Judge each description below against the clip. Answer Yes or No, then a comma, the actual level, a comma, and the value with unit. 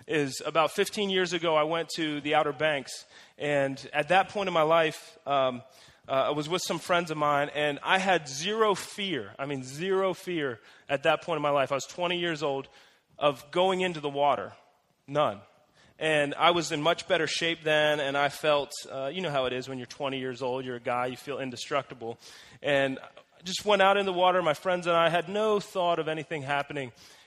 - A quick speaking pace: Yes, fast, 220 wpm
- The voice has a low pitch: No, medium, 155 Hz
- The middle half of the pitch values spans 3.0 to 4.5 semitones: Yes, average, 4.1 semitones